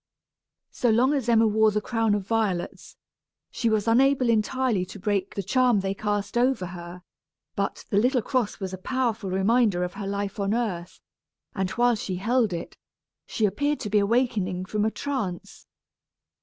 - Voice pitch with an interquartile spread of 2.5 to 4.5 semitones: Yes, average, 3.8 semitones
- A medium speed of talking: Yes, average, 170 wpm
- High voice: Yes, high, 210 Hz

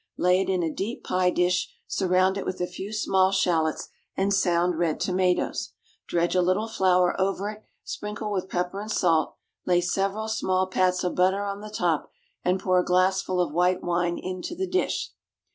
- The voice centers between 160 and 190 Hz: Yes, medium, 185 Hz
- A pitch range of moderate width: No, narrow, 1.6 semitones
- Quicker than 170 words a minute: Yes, average, 185 wpm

